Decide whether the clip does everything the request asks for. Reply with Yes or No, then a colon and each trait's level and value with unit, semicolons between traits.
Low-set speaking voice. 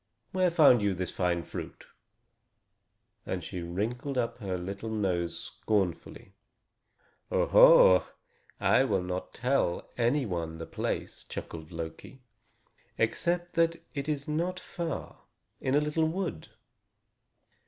Yes: low, 120 Hz